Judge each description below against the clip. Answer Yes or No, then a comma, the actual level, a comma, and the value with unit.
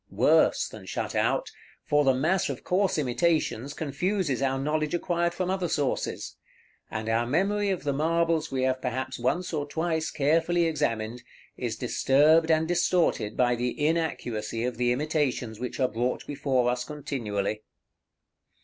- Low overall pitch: No, medium, 145 Hz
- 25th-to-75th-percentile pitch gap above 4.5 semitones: Yes, average, 5.0 semitones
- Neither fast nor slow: Yes, average, 150 wpm